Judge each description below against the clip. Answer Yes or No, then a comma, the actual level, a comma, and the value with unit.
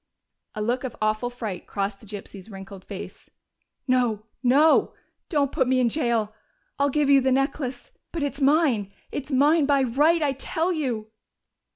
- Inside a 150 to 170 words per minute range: Yes, average, 165 wpm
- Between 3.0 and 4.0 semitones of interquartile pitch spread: No, average, 4.8 semitones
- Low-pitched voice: No, very high, 255 Hz